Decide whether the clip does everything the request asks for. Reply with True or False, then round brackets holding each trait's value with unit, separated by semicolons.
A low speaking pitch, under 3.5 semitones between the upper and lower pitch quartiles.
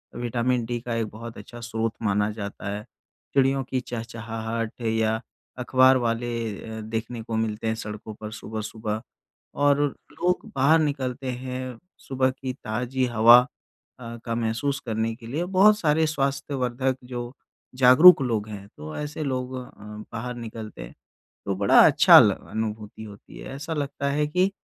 True (120 Hz; 3.1 semitones)